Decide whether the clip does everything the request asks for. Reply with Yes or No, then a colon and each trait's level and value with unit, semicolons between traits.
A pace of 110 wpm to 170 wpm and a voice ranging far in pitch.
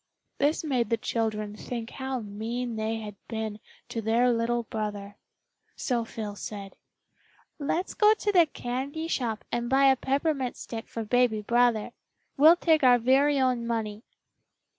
No: average, 150 wpm; average, 3.3 semitones